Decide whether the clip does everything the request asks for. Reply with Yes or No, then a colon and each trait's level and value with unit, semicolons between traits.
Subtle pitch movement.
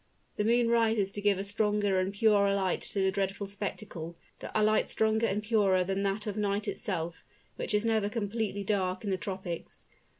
Yes: narrow, 1.8 semitones